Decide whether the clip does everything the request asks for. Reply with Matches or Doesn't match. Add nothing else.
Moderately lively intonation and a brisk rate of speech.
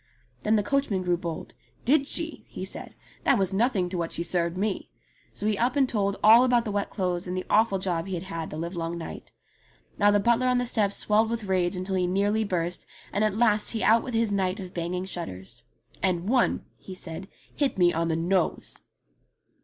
Matches